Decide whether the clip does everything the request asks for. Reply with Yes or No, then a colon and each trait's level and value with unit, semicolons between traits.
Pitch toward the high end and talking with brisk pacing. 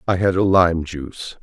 No: very low, 90 Hz; fast, 210 wpm